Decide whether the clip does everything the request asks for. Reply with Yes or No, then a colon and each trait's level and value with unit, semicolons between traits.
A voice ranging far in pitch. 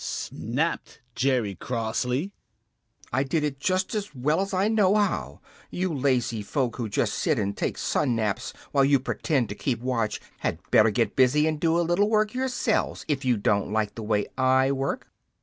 Yes: wide, 6.6 semitones